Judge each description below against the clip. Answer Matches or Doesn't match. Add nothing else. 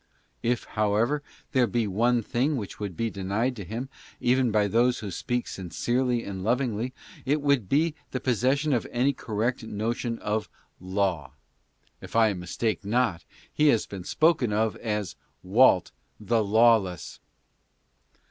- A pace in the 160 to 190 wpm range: Doesn't match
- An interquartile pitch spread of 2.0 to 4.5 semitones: Matches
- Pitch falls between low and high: Doesn't match